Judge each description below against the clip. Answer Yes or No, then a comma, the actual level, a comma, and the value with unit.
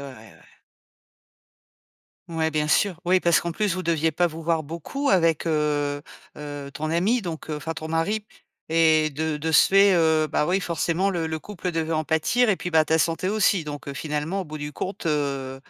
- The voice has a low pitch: No, medium, 160 Hz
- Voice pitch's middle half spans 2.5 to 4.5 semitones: Yes, average, 2.8 semitones